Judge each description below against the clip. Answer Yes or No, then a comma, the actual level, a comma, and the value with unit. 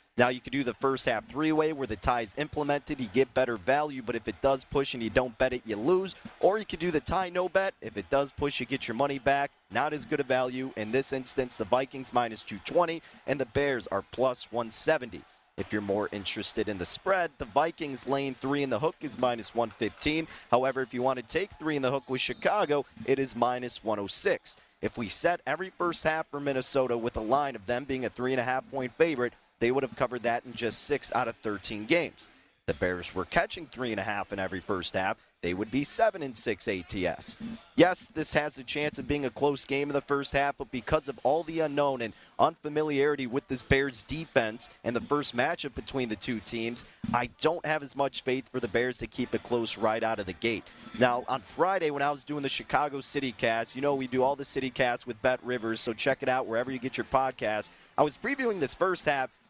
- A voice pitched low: Yes, low, 130 Hz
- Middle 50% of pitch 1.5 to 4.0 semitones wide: Yes, average, 3.1 semitones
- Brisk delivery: Yes, fast, 240 wpm